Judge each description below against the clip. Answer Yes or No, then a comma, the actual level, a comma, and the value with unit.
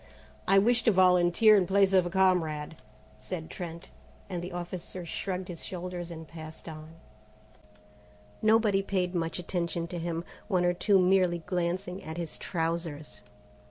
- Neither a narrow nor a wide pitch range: No, narrow, 2.1 semitones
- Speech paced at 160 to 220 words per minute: No, average, 150 wpm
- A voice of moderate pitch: Yes, medium, 175 Hz